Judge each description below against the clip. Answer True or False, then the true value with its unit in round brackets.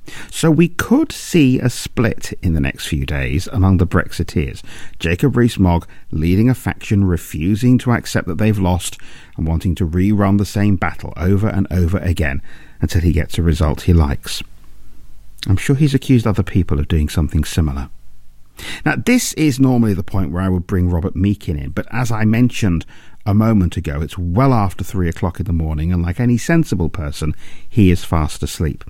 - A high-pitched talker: False (95 Hz)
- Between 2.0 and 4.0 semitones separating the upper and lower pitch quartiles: False (4.7 semitones)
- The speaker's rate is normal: True (190 wpm)